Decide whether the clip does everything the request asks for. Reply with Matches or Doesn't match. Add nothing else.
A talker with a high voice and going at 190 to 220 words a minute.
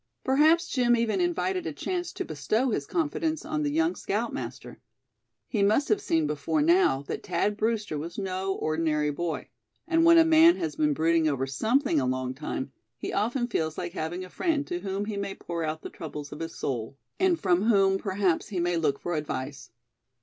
Matches